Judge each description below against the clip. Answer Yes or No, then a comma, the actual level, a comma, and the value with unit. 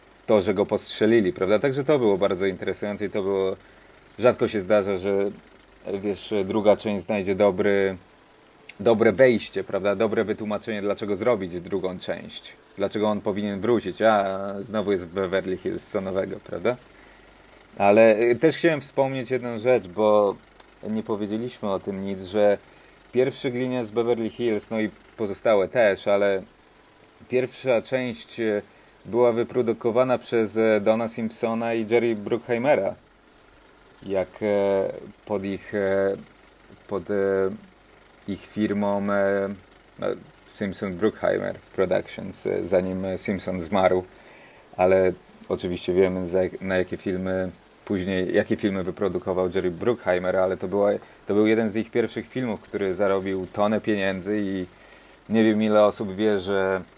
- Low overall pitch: Yes, low, 105 Hz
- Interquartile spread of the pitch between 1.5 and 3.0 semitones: Yes, narrow, 2.6 semitones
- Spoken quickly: No, average, 130 wpm